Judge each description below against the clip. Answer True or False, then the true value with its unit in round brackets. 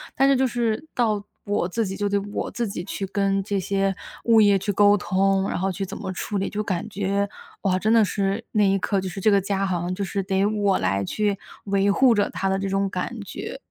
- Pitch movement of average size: False (1.4 semitones)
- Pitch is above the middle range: True (200 Hz)